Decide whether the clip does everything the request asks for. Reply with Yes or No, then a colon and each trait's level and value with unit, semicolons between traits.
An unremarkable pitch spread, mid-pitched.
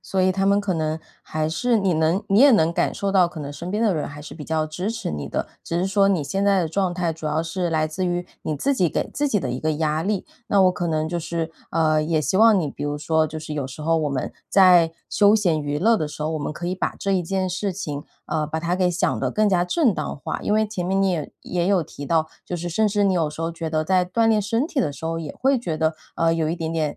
Yes: average, 3.8 semitones; medium, 170 Hz